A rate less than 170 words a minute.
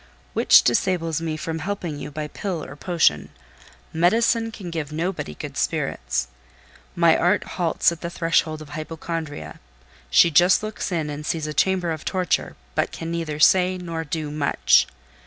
Yes: average, 160 wpm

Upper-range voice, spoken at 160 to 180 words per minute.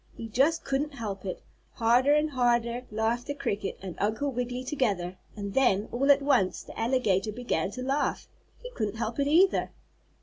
Yes: high, 240 Hz; average, 175 wpm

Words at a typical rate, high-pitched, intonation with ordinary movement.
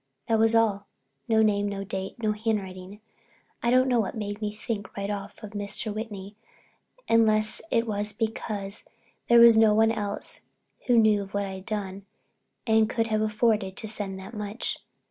No: average, 170 wpm; high, 210 Hz; narrow, 1.8 semitones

